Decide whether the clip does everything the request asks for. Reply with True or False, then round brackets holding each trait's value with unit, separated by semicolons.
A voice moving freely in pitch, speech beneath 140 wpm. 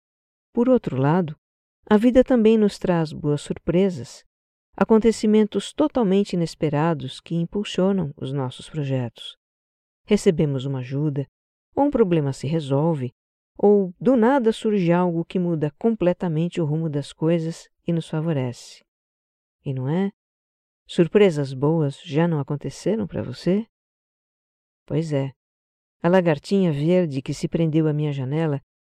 True (5.7 semitones; 130 wpm)